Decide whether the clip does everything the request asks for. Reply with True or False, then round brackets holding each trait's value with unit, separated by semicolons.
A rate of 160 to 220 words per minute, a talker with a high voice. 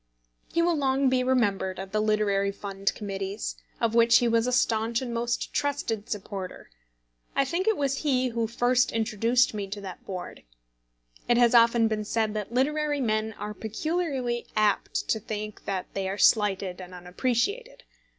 True (170 wpm; 230 Hz)